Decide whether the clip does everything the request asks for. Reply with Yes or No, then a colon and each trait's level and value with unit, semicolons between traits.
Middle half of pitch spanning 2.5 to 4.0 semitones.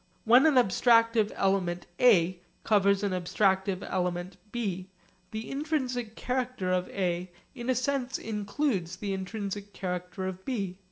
No: average, 4.6 semitones